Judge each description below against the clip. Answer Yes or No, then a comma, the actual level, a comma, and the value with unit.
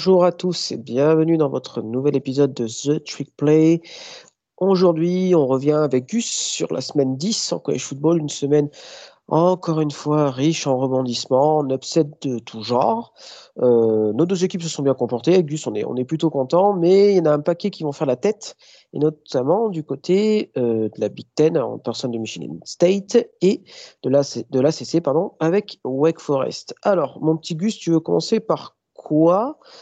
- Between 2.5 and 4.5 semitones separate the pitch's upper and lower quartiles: No, average, 5.2 semitones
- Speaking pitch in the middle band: Yes, medium, 155 Hz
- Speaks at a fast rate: No, average, 195 wpm